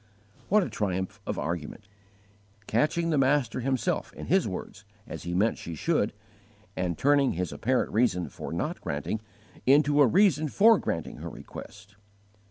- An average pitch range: No, wide, 8.1 semitones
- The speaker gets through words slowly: No, average, 155 wpm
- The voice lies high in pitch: No, low, 115 Hz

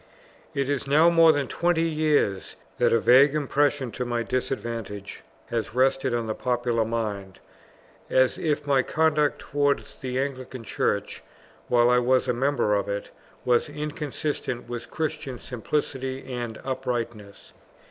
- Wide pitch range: No, average, 3.5 semitones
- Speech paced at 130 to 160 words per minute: Yes, average, 140 wpm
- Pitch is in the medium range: No, low, 130 Hz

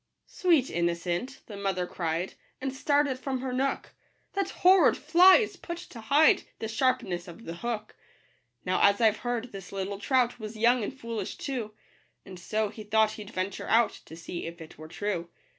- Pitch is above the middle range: Yes, high, 220 Hz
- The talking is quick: No, average, 190 wpm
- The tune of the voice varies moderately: No, wide, 5.7 semitones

